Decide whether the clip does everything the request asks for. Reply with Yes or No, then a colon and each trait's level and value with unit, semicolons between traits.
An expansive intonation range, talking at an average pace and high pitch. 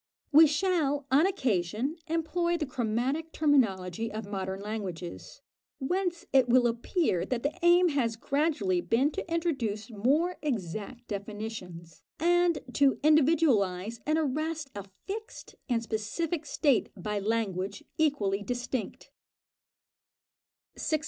No: wide, 7.1 semitones; slow, 115 wpm; very high, 255 Hz